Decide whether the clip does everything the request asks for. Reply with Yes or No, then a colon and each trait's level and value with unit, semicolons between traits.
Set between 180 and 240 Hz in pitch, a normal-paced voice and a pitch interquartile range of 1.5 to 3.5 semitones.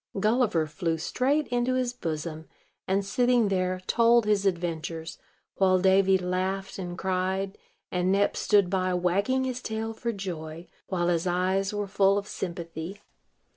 Yes: high, 190 Hz; average, 145 wpm; average, 2.9 semitones